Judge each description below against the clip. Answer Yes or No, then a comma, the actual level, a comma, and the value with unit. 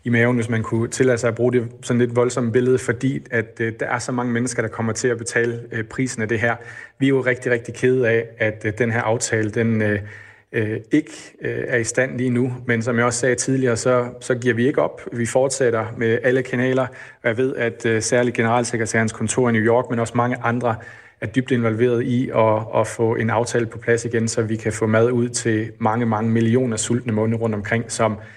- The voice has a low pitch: Yes, low, 120 Hz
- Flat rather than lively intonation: Yes, narrow, 1.6 semitones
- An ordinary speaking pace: No, fast, 240 wpm